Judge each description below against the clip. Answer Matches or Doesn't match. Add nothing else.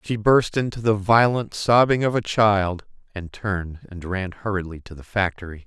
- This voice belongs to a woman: Doesn't match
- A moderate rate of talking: Matches